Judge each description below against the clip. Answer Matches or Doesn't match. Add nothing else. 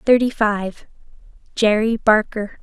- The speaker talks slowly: Matches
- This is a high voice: Matches